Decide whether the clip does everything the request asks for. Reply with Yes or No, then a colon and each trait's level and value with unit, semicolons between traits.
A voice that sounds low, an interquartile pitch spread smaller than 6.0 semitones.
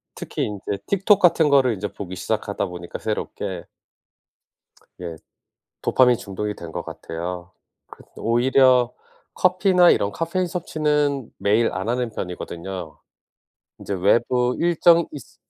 No: low, 120 Hz; wide, 8.2 semitones